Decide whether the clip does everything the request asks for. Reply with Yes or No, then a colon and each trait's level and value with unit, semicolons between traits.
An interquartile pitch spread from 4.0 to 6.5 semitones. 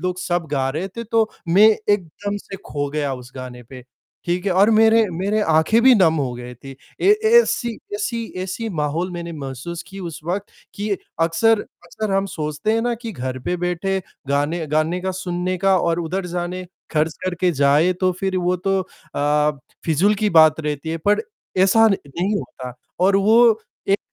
Yes: average, 4.5 semitones